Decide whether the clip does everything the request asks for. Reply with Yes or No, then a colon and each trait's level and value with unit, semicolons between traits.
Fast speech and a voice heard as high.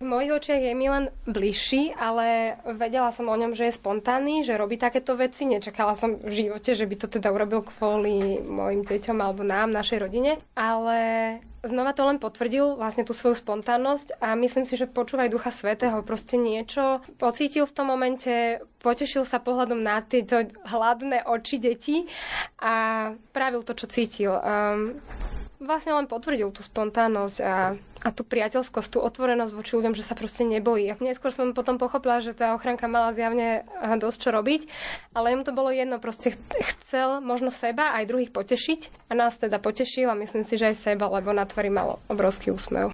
Yes: fast, 180 wpm; high, 235 Hz